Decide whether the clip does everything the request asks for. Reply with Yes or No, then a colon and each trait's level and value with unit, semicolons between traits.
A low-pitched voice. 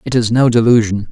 Yes: low, 115 Hz